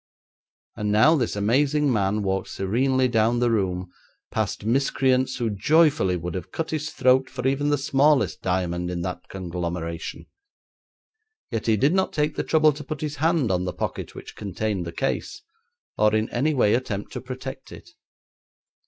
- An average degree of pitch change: No, wide, 6.4 semitones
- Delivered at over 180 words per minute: No, average, 170 wpm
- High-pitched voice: No, low, 120 Hz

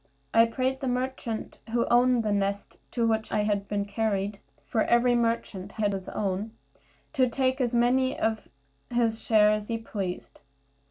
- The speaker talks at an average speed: Yes, average, 165 wpm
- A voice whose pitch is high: Yes, high, 225 Hz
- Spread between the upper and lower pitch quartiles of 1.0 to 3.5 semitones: Yes, average, 2.8 semitones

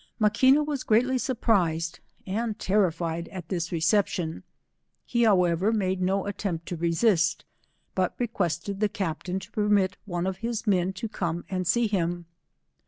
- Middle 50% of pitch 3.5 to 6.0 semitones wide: Yes, average, 3.8 semitones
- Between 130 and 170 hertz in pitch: No, high, 190 Hz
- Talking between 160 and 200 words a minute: No, average, 150 wpm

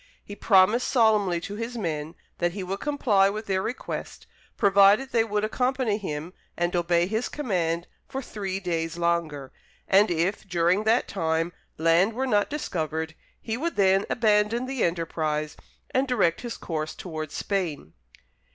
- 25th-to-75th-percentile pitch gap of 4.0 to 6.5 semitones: Yes, average, 4.7 semitones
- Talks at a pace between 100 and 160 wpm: Yes, average, 150 wpm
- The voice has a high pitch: Yes, high, 195 Hz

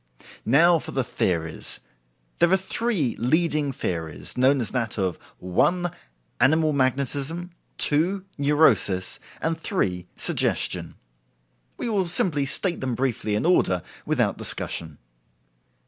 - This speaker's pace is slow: Yes, slow, 115 wpm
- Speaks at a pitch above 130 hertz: Yes, medium, 140 Hz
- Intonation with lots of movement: Yes, wide, 7.7 semitones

